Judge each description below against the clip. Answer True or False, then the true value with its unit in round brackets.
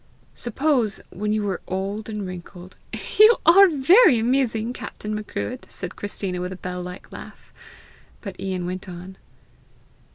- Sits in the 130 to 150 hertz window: False (205 Hz)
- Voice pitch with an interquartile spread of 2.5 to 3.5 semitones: False (5.0 semitones)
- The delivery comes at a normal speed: True (150 wpm)